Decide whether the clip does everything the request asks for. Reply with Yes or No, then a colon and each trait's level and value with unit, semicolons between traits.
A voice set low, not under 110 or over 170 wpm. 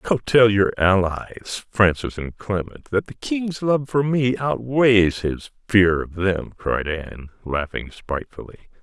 Yes: low, 105 Hz; average, 150 wpm